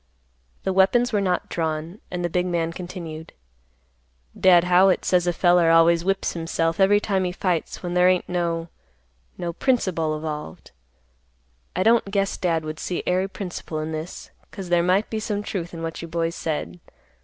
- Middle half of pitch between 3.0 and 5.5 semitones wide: No, narrow, 2.4 semitones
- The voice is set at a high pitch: No, medium, 175 Hz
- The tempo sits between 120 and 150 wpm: No, average, 170 wpm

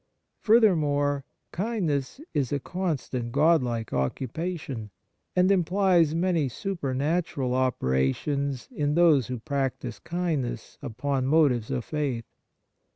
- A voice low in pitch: No, medium, 145 Hz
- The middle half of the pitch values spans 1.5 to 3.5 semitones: No, average, 5.1 semitones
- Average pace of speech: No, slow, 105 wpm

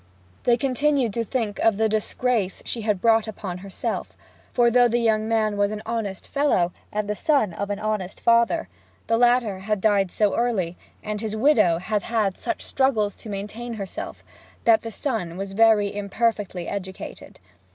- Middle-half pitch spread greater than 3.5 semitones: No, narrow, 2.6 semitones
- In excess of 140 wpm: Yes, average, 170 wpm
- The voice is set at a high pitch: Yes, high, 215 Hz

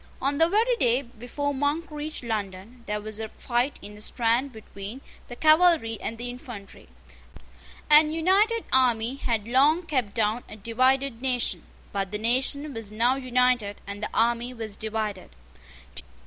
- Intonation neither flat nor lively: Yes, average, 4.3 semitones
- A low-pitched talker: No, high, 245 Hz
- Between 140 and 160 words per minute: Yes, average, 155 wpm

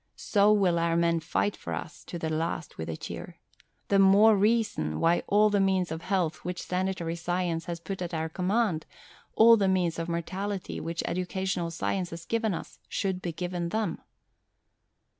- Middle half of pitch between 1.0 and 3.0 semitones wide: Yes, average, 2.7 semitones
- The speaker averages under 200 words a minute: Yes, average, 180 wpm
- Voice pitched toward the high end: No, medium, 180 Hz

